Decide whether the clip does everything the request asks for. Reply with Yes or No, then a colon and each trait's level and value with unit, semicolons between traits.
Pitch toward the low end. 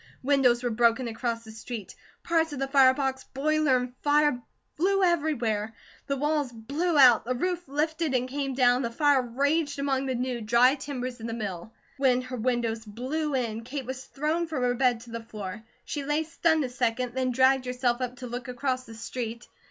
No: very high, 255 Hz